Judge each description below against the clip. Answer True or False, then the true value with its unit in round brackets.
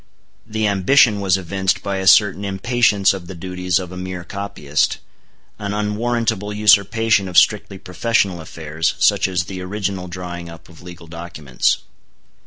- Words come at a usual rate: True (150 wpm)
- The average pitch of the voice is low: True (95 Hz)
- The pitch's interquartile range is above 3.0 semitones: False (2.6 semitones)